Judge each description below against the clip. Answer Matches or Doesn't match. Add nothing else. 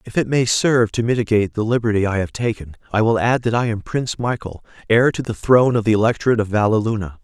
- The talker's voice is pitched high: Doesn't match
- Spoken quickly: Matches